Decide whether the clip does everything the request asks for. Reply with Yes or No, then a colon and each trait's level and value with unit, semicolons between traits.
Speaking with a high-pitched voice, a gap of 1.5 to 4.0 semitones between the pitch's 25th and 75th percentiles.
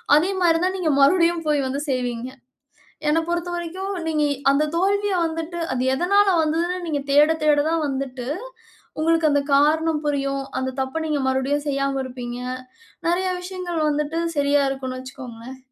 Yes: very high, 300 Hz; average, 3.7 semitones